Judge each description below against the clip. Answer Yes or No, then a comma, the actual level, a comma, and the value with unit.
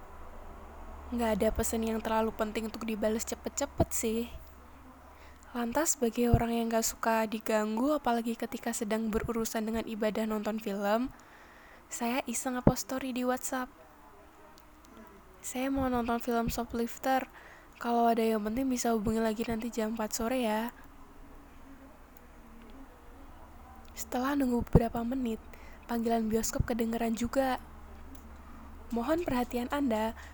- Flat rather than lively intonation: Yes, narrow, 1.7 semitones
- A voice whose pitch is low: No, high, 230 Hz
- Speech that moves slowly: No, average, 115 wpm